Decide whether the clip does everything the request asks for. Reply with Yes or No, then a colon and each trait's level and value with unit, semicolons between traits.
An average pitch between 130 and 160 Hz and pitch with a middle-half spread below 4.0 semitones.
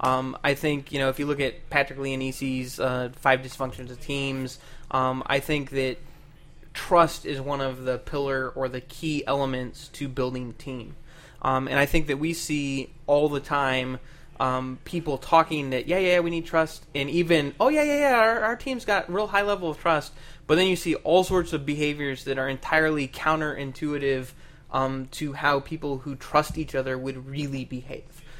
Yes: medium, 140 Hz; average, 2.9 semitones